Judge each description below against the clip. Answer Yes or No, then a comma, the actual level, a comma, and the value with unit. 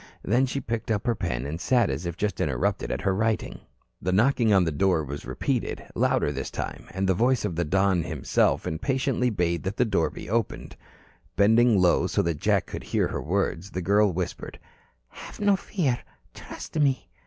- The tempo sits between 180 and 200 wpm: Yes, average, 195 wpm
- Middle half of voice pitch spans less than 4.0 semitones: No, wide, 5.6 semitones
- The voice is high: No, low, 100 Hz